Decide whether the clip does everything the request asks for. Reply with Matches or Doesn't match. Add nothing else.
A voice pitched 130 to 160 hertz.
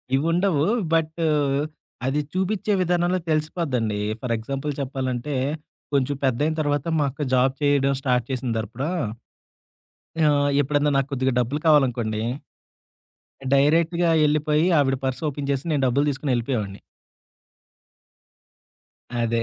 Matches